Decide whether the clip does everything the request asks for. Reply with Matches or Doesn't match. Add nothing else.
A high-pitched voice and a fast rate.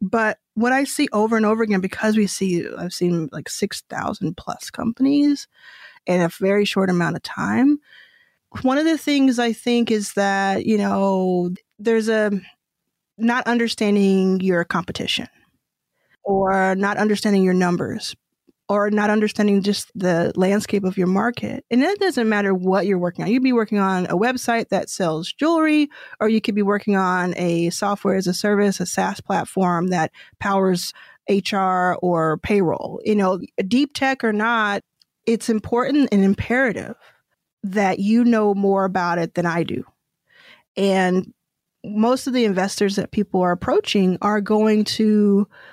Doesn't match